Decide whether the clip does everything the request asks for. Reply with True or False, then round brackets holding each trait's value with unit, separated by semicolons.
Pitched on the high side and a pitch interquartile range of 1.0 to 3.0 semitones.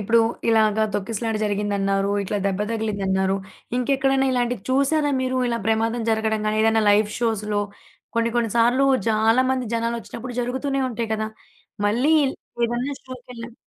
True (230 Hz; 2.7 semitones)